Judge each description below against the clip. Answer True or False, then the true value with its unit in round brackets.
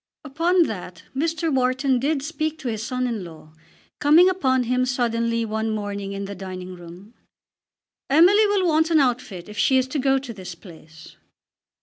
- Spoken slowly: False (175 wpm)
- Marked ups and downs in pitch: True (6.8 semitones)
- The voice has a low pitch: False (250 Hz)